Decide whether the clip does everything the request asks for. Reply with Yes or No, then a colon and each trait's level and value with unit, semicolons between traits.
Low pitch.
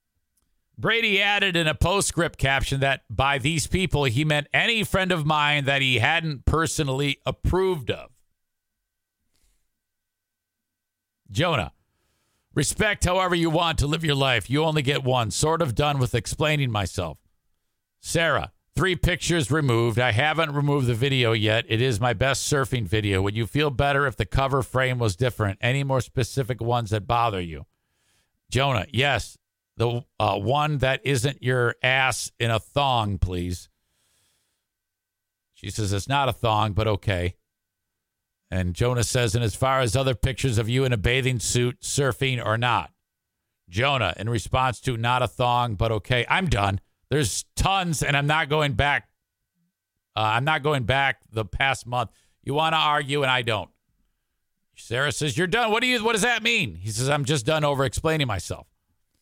Yes: low, 125 Hz